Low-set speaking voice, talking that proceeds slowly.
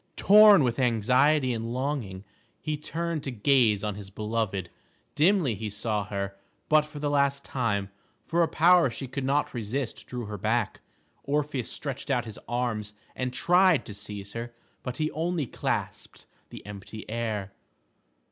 No: low, 125 Hz; average, 155 wpm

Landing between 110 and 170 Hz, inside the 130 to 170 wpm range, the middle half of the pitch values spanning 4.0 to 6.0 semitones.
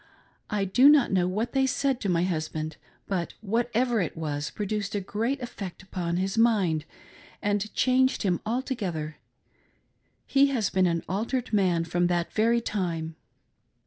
No: high, 200 Hz; average, 160 wpm; average, 5.3 semitones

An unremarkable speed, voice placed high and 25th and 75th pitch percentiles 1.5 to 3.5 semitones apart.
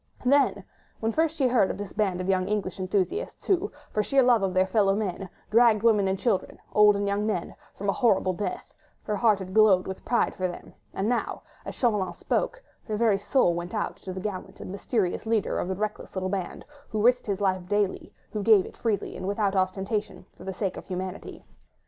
No: fast, 215 wpm; high, 205 Hz; average, 2.8 semitones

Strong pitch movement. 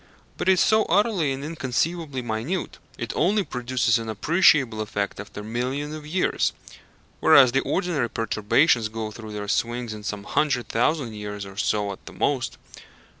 Yes: wide, 6.2 semitones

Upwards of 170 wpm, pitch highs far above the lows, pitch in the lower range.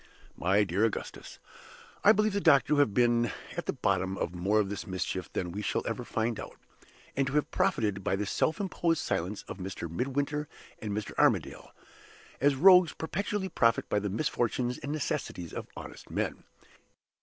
Yes: average, 180 wpm; wide, 7.2 semitones; low, 115 Hz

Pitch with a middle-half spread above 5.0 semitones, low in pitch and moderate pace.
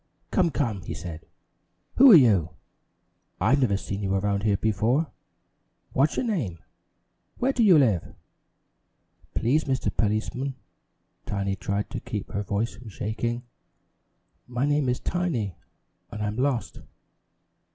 No: wide, 5.6 semitones; low, 115 Hz; slow, 130 wpm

